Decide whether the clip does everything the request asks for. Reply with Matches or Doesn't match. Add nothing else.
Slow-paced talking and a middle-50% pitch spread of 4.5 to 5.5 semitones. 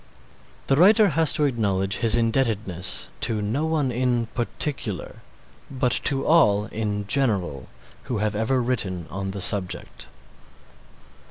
Matches